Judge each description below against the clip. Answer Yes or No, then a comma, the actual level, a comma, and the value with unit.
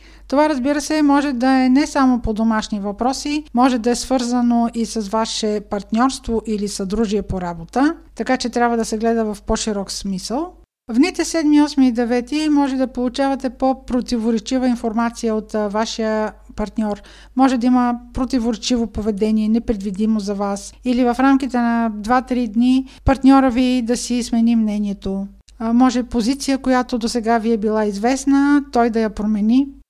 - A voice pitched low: No, high, 240 Hz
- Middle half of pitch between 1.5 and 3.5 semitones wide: Yes, average, 3.0 semitones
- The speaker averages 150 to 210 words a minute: Yes, average, 160 wpm